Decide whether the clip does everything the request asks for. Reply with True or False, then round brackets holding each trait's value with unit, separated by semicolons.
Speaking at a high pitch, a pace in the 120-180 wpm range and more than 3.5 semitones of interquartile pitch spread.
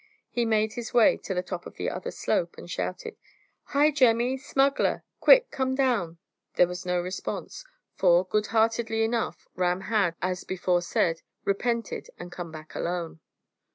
True (210 Hz; 160 wpm; 5.1 semitones)